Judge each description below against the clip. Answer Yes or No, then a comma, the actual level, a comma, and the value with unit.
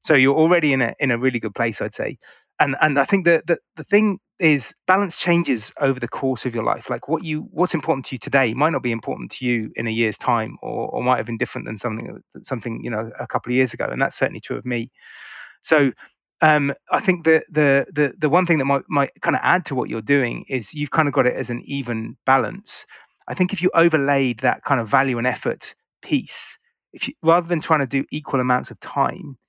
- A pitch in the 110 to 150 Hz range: Yes, medium, 140 Hz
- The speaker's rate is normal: No, fast, 250 wpm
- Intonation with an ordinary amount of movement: Yes, average, 4.3 semitones